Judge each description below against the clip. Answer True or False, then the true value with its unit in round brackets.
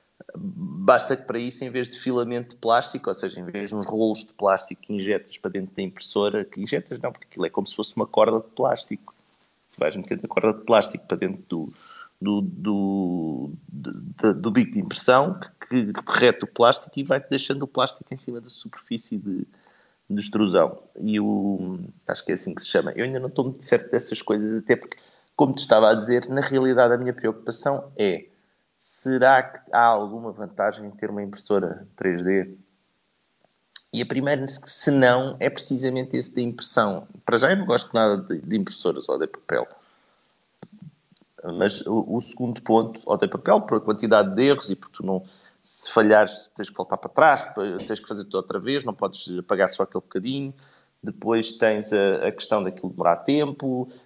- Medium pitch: False (120 Hz)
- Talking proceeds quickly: True (195 wpm)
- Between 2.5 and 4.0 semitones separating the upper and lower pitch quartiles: False (4.5 semitones)